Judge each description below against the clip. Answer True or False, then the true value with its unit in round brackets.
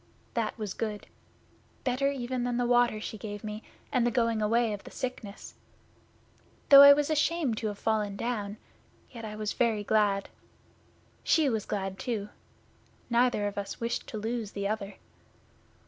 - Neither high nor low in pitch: False (220 Hz)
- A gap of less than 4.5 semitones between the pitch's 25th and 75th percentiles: True (2.8 semitones)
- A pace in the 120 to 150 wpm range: False (160 wpm)